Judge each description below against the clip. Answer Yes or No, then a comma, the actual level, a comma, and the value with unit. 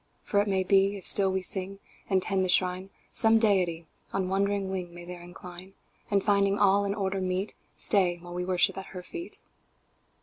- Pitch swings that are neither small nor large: No, narrow, 1.7 semitones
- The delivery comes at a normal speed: Yes, average, 195 wpm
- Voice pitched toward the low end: No, high, 190 Hz